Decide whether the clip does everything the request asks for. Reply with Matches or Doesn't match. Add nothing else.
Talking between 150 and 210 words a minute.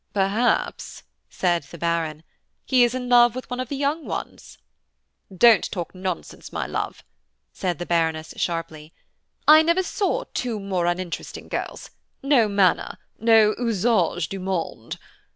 Doesn't match